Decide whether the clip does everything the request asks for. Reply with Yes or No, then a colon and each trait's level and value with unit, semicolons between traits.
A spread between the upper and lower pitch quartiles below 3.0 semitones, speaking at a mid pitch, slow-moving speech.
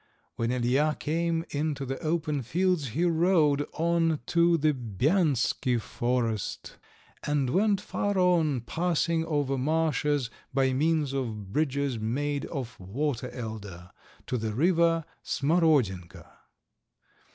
No: average, 4.7 semitones; medium, 145 Hz; slow, 115 wpm